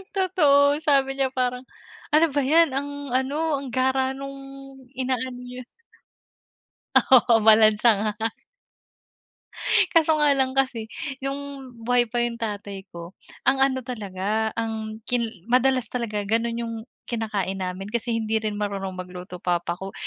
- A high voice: Yes, high, 240 Hz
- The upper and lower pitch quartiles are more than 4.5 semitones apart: No, average, 4.0 semitones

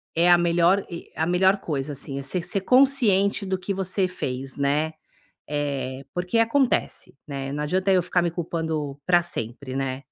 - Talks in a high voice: No, medium, 170 Hz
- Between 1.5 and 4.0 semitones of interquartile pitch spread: No, average, 5.1 semitones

